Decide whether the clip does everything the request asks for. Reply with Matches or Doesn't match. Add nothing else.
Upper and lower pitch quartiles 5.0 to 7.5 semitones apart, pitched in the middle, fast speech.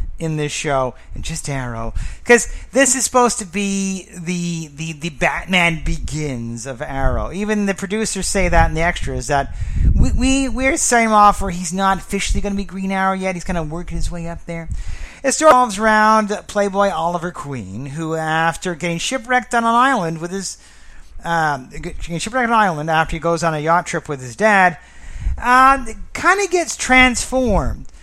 Doesn't match